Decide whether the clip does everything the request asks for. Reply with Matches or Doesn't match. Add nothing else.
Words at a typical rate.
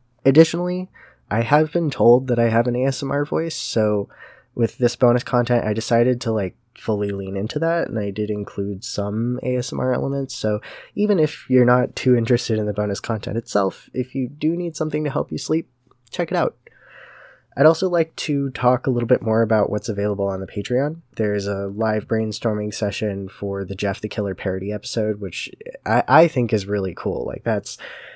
Matches